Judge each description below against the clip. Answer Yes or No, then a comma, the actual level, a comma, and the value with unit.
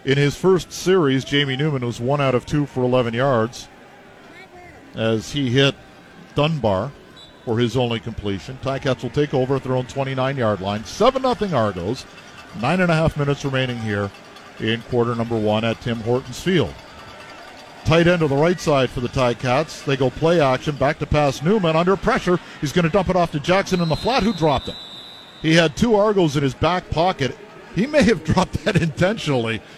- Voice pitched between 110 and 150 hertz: Yes, medium, 140 Hz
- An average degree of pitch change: No, wide, 5.7 semitones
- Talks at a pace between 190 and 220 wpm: Yes, average, 195 wpm